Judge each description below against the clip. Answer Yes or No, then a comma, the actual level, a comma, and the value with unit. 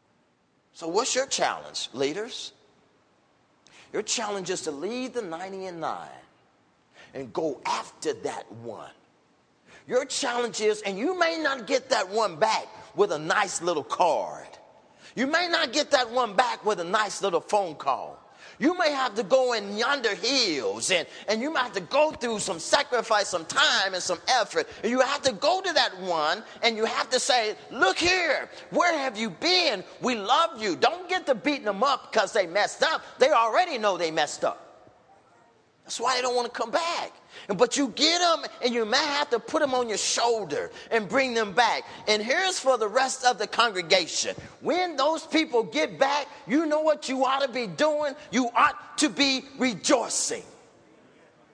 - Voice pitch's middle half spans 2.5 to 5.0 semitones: No, wide, 5.6 semitones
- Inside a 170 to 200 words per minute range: Yes, average, 185 wpm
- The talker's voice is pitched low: No, very high, 255 Hz